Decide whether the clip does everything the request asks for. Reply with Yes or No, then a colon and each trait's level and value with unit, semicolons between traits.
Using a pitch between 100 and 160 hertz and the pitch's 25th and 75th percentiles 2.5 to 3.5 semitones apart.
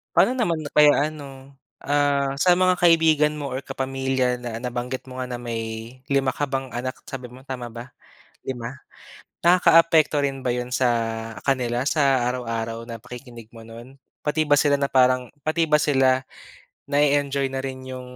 Yes: low, 135 Hz; average, 2.8 semitones